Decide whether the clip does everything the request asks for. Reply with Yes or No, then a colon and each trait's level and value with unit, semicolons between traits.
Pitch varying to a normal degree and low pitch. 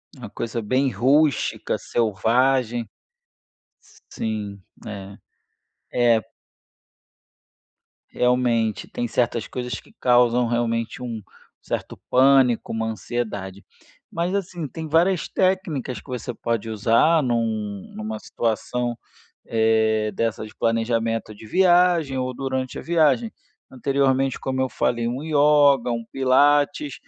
Yes: average, 3.5 semitones; low, 125 Hz